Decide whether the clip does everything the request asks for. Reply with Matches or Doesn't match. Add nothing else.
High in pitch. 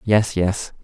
Doesn't match